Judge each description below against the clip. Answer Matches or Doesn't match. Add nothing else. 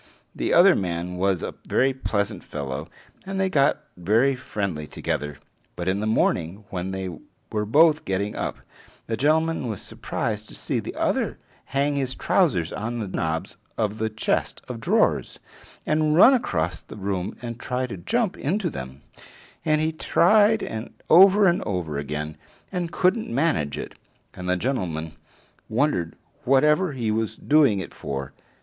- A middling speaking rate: Matches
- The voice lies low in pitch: Matches